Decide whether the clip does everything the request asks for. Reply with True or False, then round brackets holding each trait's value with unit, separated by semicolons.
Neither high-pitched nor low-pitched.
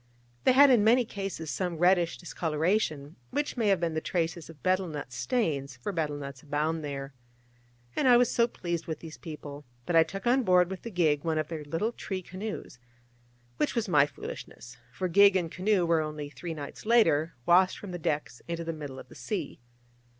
True (165 Hz)